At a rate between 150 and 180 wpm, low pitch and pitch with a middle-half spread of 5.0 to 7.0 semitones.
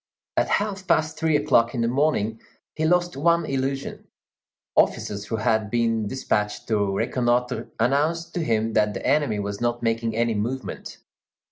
Yes: average, 155 wpm; low, 120 Hz; wide, 5.4 semitones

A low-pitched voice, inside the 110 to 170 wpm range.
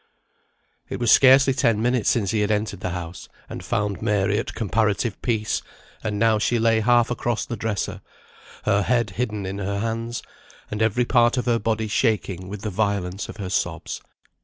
No: low, 110 Hz; average, 185 wpm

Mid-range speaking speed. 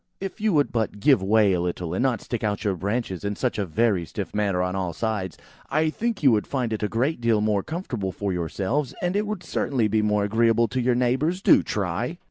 No: fast, 235 wpm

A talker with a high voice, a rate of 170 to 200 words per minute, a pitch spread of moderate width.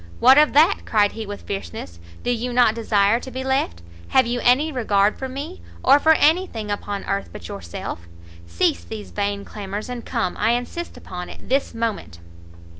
Yes: high, 225 Hz; average, 190 wpm; average, 4.6 semitones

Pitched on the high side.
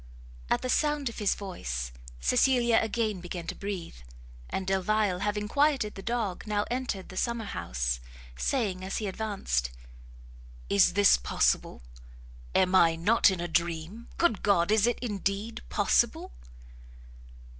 Yes: high, 200 Hz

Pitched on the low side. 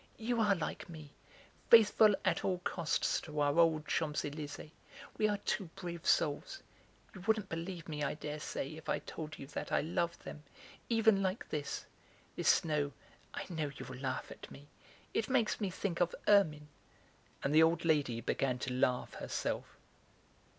No: medium, 160 Hz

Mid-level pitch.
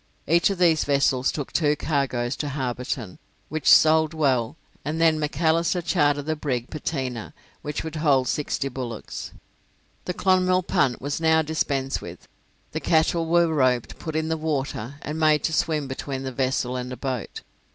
Yes: medium, 150 Hz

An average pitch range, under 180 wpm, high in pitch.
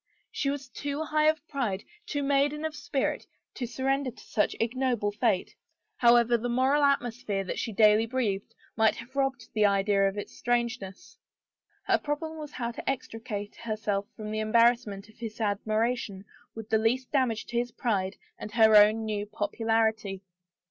Yes: average, 3.6 semitones; average, 165 wpm; high, 230 Hz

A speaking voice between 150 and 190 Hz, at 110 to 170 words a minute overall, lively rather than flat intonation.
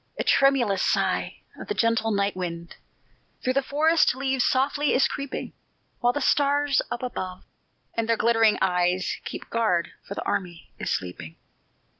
No: high, 230 Hz; average, 155 wpm; wide, 6.6 semitones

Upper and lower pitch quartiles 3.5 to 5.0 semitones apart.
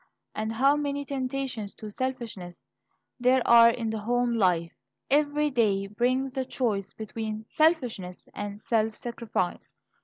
Yes: average, 3.8 semitones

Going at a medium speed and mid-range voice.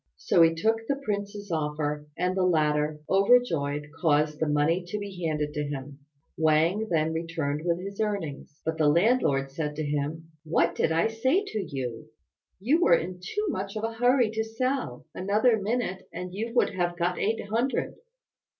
Yes: average, 175 wpm; medium, 175 Hz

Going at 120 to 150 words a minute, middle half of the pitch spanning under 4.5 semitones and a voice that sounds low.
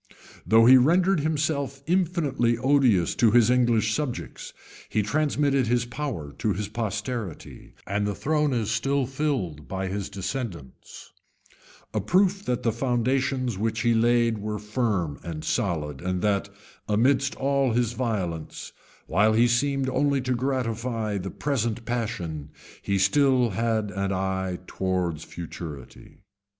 No: slow, 135 wpm; average, 5.1 semitones; low, 115 Hz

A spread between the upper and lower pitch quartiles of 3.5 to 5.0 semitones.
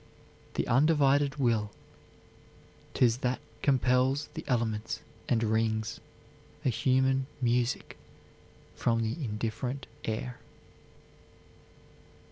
No: average, 2.8 semitones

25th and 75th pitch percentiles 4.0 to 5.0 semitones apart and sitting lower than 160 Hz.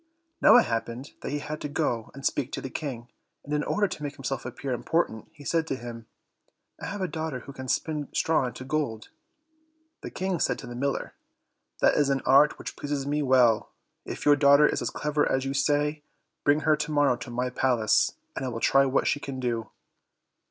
No: average, 2.9 semitones; medium, 140 Hz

